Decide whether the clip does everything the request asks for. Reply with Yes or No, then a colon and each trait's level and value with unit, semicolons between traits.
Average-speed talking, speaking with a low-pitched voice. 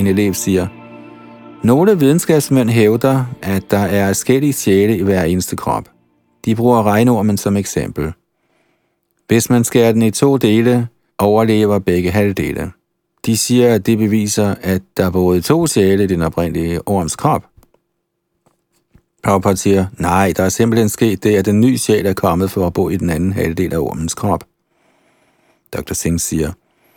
Yes: average, 160 wpm; low, 100 Hz